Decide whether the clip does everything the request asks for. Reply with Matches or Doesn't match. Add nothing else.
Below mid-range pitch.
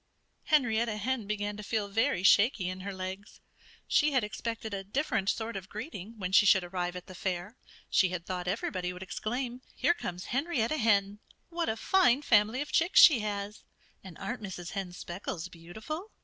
Doesn't match